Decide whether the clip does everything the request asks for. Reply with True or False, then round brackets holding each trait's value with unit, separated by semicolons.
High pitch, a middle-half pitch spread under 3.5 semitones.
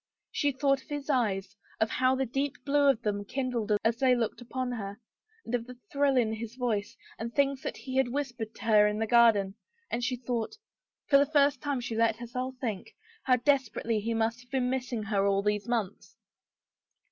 True (245 Hz; 3.1 semitones)